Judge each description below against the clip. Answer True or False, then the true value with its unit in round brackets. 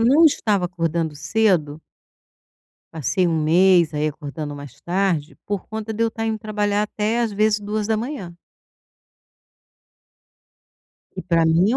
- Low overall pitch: False (190 Hz)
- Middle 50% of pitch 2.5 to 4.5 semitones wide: False (4.9 semitones)